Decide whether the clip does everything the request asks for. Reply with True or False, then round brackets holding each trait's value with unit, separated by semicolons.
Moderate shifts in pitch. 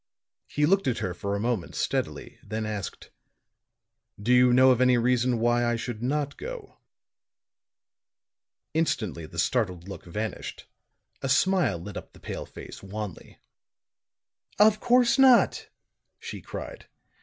False (5.9 semitones)